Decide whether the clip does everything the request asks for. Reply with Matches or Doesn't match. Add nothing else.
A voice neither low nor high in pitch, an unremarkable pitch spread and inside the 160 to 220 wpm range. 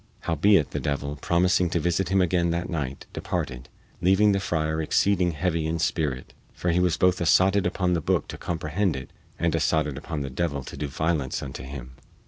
Doesn't match